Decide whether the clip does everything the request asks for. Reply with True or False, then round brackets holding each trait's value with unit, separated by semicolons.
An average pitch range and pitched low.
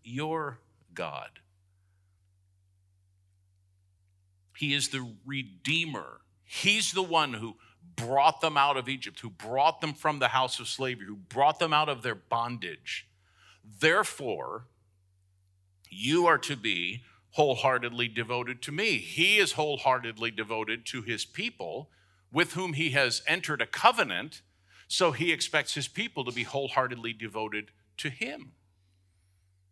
False (7.3 semitones; 115 Hz)